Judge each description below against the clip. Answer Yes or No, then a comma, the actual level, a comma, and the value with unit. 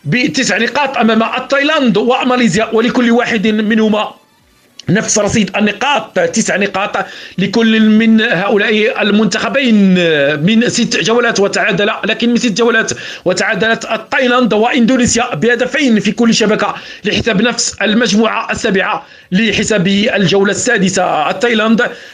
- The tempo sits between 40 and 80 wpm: No, average, 110 wpm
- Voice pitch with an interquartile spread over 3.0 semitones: No, narrow, 2.4 semitones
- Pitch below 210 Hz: No, high, 220 Hz